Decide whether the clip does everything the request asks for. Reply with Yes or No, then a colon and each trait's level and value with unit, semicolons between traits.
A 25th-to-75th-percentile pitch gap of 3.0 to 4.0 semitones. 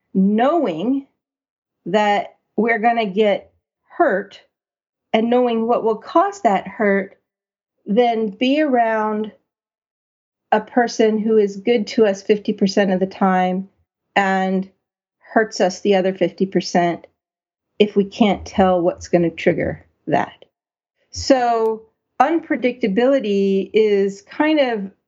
Yes: average, 3.6 semitones